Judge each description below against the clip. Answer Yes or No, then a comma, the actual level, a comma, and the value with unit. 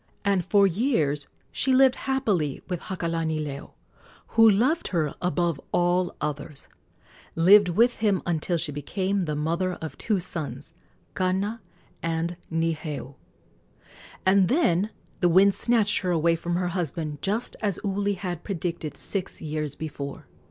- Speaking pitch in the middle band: Yes, medium, 175 Hz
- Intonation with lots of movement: No, average, 4.0 semitones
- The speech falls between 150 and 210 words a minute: No, slow, 135 wpm